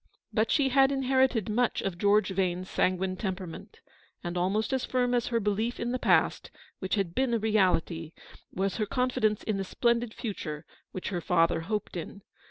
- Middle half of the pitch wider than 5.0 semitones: No, average, 4.6 semitones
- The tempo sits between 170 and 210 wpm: Yes, average, 180 wpm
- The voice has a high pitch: Yes, high, 210 Hz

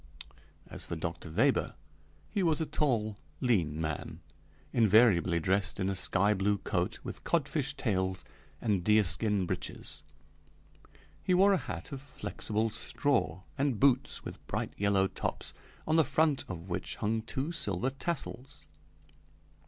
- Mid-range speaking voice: No, low, 110 Hz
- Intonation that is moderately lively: No, wide, 6.7 semitones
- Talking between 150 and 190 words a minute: No, slow, 135 wpm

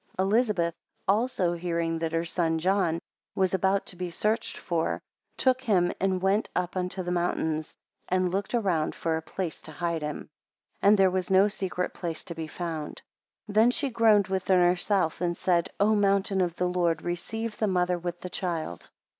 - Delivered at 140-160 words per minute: No, average, 190 wpm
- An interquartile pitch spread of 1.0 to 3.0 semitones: Yes, average, 2.7 semitones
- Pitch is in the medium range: Yes, medium, 180 Hz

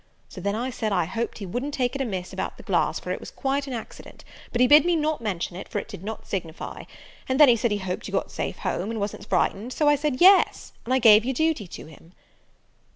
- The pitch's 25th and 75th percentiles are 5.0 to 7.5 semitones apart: Yes, wide, 5.4 semitones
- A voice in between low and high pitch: No, high, 235 Hz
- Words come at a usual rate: No, fast, 260 wpm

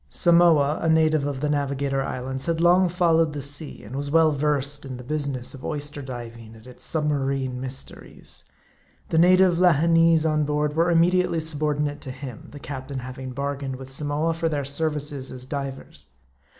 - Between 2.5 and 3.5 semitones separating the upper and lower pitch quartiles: Yes, average, 3.1 semitones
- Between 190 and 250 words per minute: No, average, 175 wpm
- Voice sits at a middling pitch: Yes, medium, 145 Hz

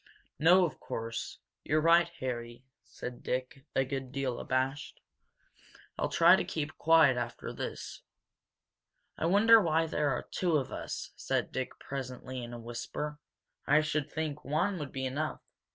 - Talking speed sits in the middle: Yes, average, 155 wpm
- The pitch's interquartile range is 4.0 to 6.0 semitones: No, average, 3.5 semitones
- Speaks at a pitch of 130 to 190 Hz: Yes, medium, 140 Hz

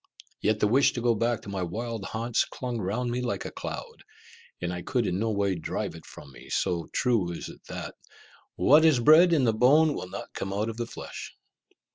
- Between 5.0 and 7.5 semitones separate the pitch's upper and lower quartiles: No, average, 4.1 semitones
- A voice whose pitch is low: Yes, low, 115 Hz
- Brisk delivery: Yes, fast, 220 wpm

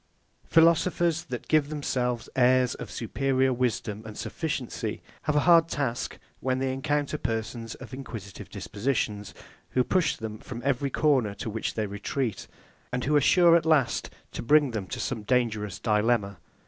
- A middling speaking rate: Yes, average, 160 wpm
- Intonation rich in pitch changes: No, average, 4.5 semitones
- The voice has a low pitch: Yes, low, 125 Hz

